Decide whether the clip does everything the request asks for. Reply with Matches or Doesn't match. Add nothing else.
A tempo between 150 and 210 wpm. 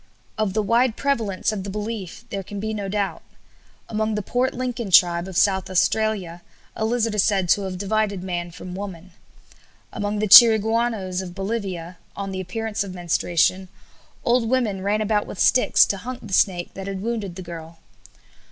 Matches